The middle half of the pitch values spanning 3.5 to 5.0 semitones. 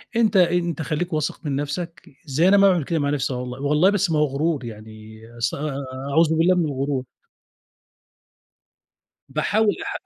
Yes: average, 4.2 semitones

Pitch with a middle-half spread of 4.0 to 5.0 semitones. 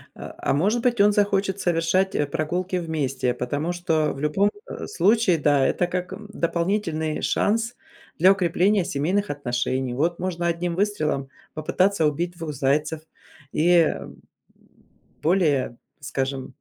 Yes: average, 4.5 semitones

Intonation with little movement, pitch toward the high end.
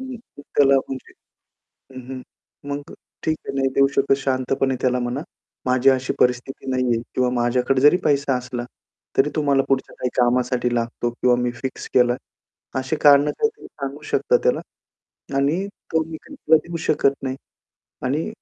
No: narrow, 2.3 semitones; low, 135 Hz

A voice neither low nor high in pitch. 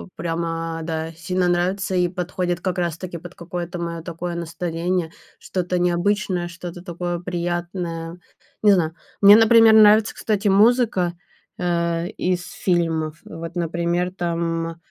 Yes: medium, 175 Hz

